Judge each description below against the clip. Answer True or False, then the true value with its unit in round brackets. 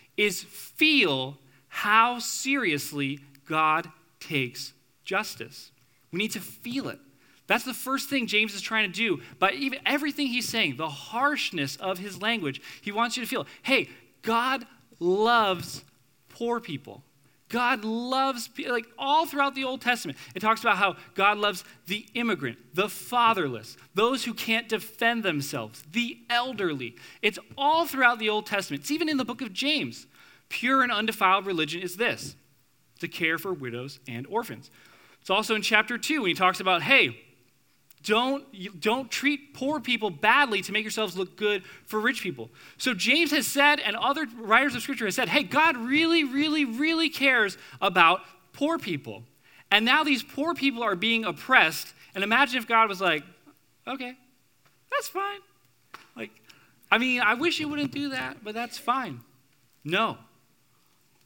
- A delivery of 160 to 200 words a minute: True (165 wpm)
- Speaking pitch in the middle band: False (220 Hz)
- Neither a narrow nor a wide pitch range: False (7.5 semitones)